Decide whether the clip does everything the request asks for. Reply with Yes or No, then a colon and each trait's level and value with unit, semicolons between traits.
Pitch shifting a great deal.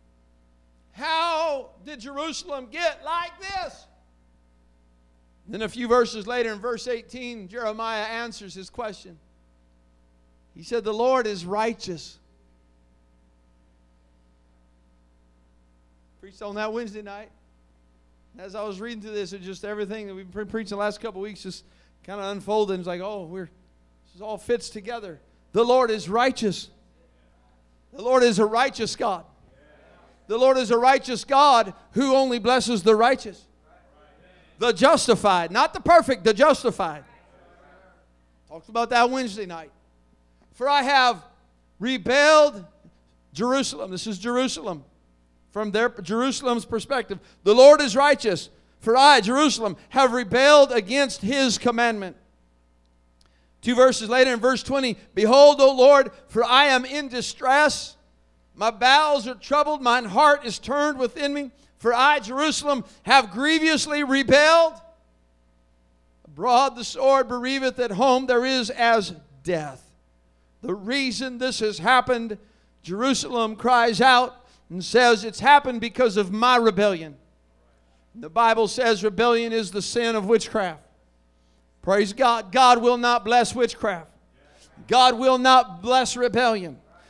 Yes: wide, 8.2 semitones